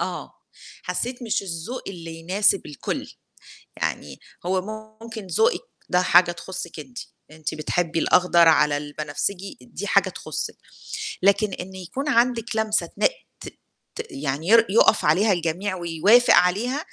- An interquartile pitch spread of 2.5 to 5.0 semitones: No, wide, 5.5 semitones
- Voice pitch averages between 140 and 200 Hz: Yes, medium, 185 Hz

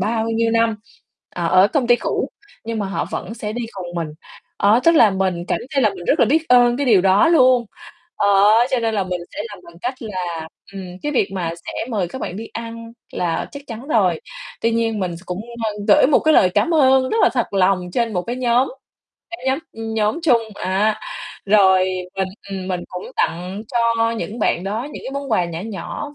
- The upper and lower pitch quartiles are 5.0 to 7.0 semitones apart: No, average, 4.3 semitones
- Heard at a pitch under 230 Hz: Yes, high, 220 Hz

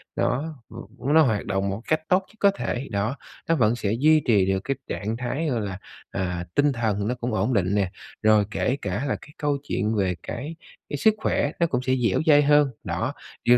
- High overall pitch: No, low, 120 Hz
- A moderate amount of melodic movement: No, wide, 6.1 semitones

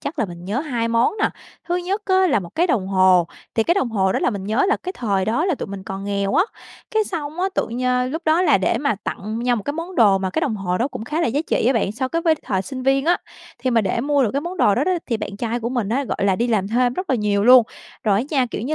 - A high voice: Yes, high, 245 Hz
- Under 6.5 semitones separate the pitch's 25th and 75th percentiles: No, wide, 6.8 semitones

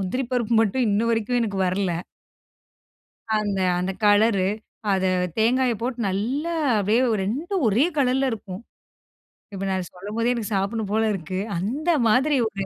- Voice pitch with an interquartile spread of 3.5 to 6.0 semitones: Yes, average, 4.2 semitones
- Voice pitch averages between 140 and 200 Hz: No, high, 220 Hz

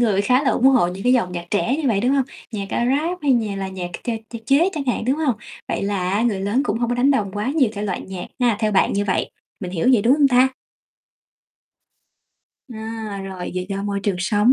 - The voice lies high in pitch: Yes, high, 220 Hz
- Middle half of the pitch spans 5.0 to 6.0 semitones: No, average, 4.5 semitones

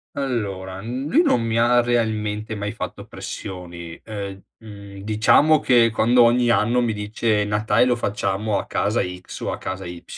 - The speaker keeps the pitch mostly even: No, average, 3.2 semitones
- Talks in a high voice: No, low, 110 Hz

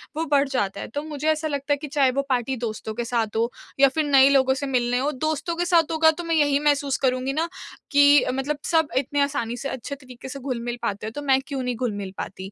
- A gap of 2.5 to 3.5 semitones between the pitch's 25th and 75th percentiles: Yes, average, 2.9 semitones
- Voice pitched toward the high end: Yes, very high, 275 Hz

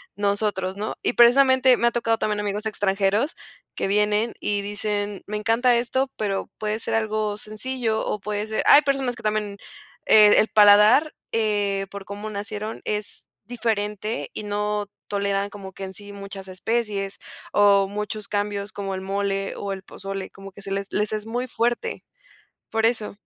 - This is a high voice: Yes, high, 210 Hz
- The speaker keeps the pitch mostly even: Yes, narrow, 1.6 semitones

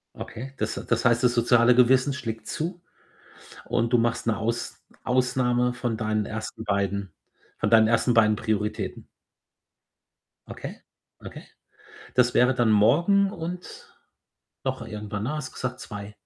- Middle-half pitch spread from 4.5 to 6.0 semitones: No, narrow, 2.6 semitones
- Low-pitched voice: Yes, low, 120 Hz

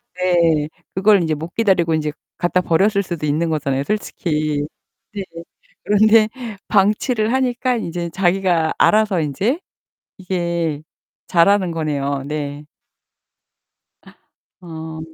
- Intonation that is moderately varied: Yes, average, 4.3 semitones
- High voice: No, medium, 170 Hz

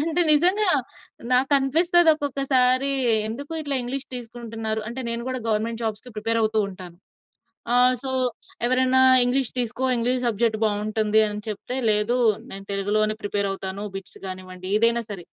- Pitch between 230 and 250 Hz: Yes, high, 235 Hz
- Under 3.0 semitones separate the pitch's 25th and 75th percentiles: No, average, 3.6 semitones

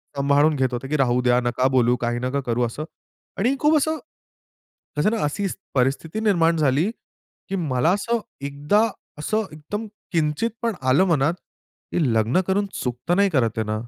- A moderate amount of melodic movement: No, wide, 7.3 semitones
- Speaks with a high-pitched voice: No, medium, 150 Hz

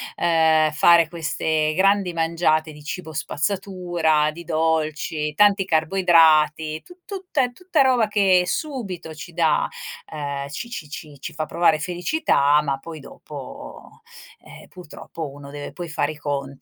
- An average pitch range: Yes, average, 3.1 semitones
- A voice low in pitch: No, medium, 160 Hz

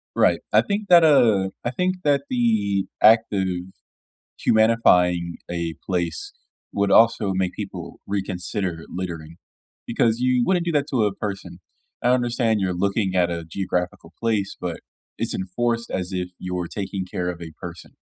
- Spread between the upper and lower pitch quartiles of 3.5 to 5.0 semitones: Yes, average, 4.6 semitones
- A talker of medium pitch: No, low, 100 Hz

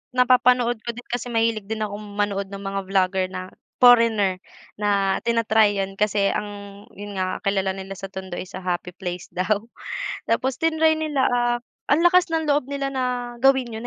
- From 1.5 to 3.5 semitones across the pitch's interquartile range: No, average, 4.1 semitones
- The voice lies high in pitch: Yes, high, 215 Hz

